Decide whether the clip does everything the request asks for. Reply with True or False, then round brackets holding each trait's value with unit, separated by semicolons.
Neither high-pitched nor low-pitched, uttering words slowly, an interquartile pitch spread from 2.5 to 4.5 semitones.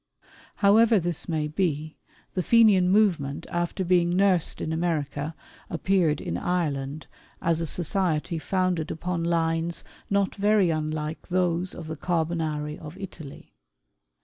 True (170 Hz; 125 wpm; 2.9 semitones)